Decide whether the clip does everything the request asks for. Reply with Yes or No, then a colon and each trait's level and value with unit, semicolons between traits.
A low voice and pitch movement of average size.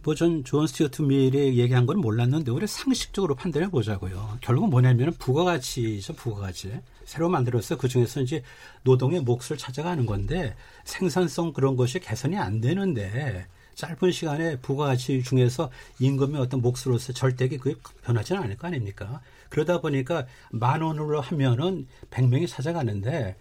Yes: low, 130 Hz; average, 4.4 semitones